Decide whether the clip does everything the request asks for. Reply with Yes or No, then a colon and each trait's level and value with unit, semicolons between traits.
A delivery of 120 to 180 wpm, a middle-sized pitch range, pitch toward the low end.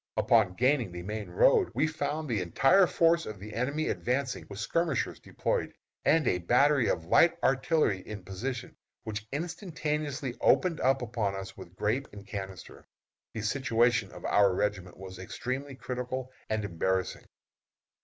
No: average, 145 wpm; wide, 6.2 semitones; low, 120 Hz